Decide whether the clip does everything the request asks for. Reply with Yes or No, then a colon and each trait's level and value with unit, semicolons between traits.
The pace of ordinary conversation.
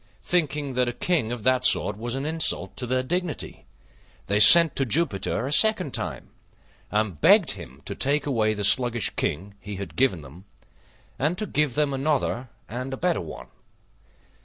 Yes: average, 175 wpm